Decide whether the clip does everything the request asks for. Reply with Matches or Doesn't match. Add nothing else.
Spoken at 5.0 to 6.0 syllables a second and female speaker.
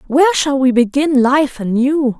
Doesn't match